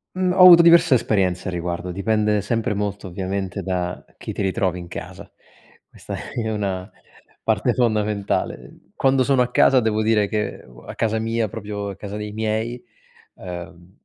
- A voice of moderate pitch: No, low, 105 Hz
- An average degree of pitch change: Yes, average, 3.2 semitones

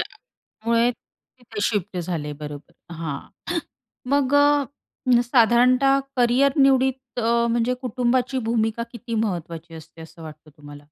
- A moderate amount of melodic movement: No, wide, 7.4 semitones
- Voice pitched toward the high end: Yes, high, 235 Hz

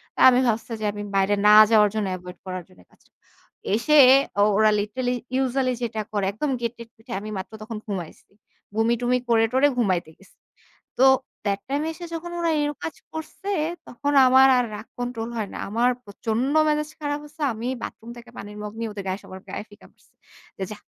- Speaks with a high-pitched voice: Yes, high, 230 Hz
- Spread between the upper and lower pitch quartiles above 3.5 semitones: Yes, average, 3.9 semitones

